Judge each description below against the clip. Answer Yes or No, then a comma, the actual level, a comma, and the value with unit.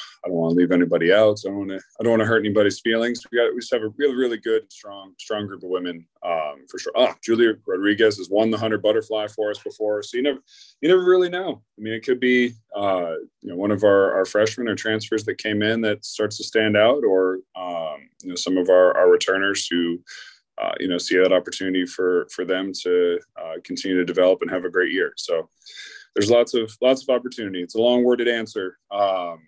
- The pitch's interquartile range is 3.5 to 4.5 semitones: Yes, average, 3.9 semitones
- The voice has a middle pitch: No, low, 105 Hz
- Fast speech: Yes, fast, 240 wpm